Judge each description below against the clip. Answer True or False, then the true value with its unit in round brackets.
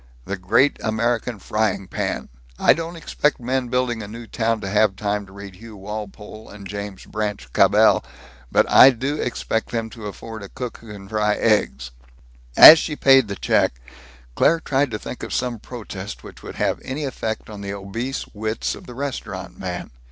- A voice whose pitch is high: False (110 Hz)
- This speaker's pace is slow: False (185 wpm)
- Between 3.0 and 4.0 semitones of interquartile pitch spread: True (3.4 semitones)